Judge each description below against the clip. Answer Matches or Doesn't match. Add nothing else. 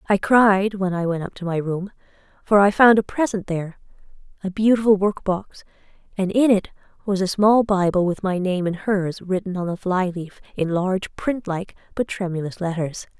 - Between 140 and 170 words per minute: Doesn't match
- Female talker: Matches